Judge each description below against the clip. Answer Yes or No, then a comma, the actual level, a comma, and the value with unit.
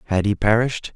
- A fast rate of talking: No, average, 190 wpm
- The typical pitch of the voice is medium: No, low, 110 Hz